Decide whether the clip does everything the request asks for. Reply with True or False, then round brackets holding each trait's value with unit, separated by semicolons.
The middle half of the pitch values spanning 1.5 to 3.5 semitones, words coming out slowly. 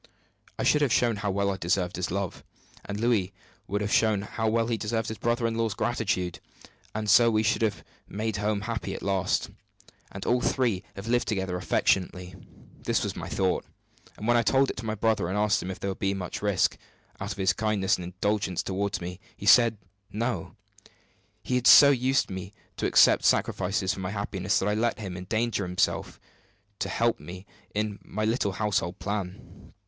False (2.9 semitones; 195 wpm)